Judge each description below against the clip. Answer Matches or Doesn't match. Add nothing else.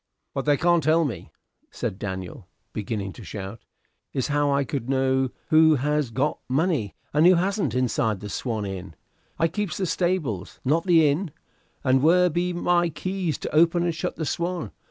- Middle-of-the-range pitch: Matches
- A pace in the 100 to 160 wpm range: Doesn't match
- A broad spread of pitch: Matches